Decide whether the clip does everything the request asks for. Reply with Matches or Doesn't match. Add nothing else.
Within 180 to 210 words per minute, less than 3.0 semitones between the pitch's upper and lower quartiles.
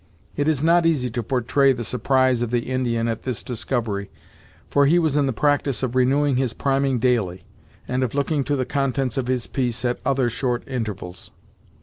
Matches